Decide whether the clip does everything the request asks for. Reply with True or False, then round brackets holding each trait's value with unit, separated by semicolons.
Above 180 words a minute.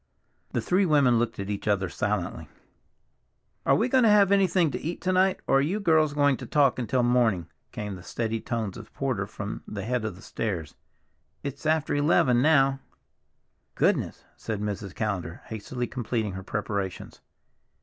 False (170 wpm)